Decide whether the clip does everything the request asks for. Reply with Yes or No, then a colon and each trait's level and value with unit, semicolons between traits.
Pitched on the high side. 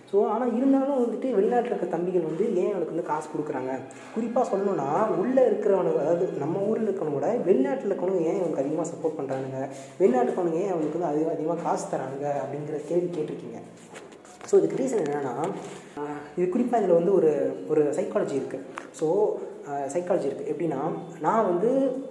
No: medium, 180 Hz